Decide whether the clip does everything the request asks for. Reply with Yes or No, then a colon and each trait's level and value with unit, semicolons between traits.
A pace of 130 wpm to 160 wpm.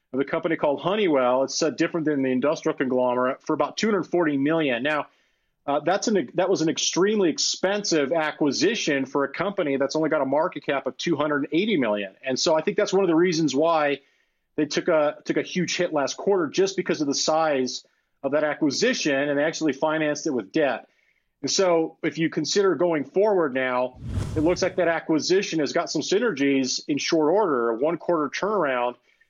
No: average, 195 wpm